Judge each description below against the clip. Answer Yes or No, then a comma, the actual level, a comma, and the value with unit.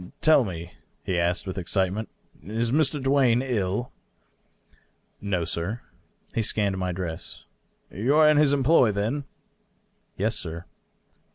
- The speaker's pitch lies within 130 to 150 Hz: No, low, 105 Hz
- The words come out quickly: No, average, 155 wpm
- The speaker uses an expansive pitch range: Yes, wide, 6.3 semitones